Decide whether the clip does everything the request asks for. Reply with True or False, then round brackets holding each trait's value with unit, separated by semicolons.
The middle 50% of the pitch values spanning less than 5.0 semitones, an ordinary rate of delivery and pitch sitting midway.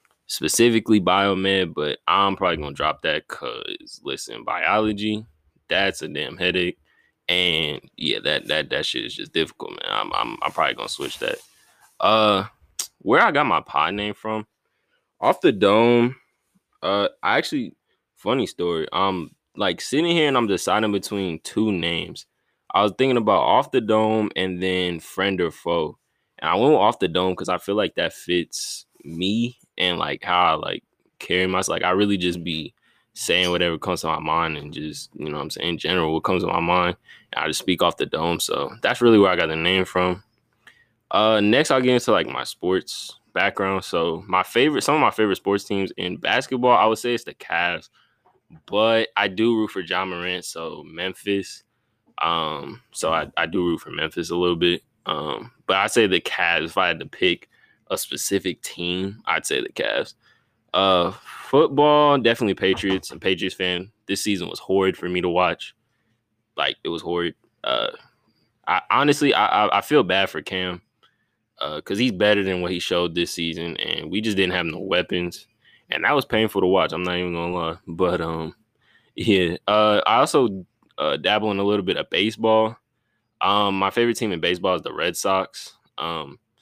False (3.7 semitones; 190 wpm; 95 Hz)